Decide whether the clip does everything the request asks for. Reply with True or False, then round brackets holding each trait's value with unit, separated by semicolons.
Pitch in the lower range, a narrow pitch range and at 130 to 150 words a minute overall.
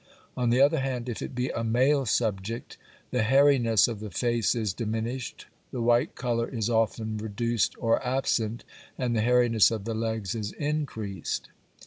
False (115 Hz; 2.1 semitones; 165 wpm)